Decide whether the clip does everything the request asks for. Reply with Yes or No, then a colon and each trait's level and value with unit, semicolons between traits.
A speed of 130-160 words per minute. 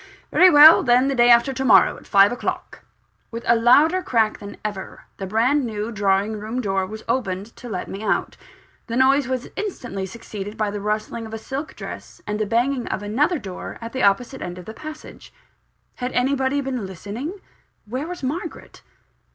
No: average, 185 wpm